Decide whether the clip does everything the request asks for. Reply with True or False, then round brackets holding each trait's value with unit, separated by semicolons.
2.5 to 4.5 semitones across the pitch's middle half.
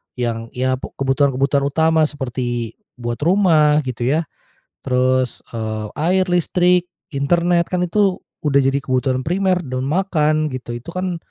False (5.2 semitones)